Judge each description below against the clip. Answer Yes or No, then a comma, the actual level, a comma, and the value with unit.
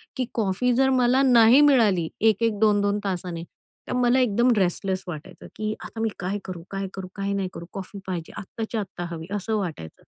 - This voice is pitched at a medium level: No, high, 205 Hz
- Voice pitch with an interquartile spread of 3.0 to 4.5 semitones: Yes, average, 3.9 semitones